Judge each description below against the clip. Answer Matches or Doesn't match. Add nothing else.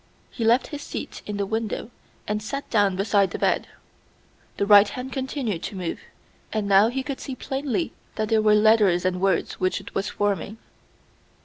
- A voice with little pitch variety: Doesn't match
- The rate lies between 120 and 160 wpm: Doesn't match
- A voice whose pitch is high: Matches